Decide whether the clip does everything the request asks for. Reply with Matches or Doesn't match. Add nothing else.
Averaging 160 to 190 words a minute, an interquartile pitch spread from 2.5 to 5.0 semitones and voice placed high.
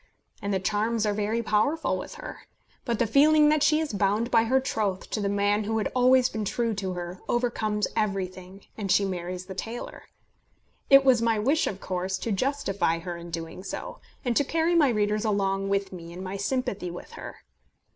Doesn't match